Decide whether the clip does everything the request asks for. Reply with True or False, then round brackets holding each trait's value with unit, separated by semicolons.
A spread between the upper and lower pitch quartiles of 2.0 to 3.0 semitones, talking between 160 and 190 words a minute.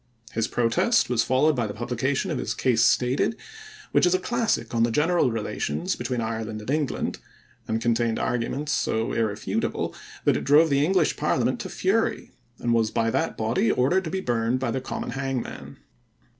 False (4.2 semitones; 180 wpm)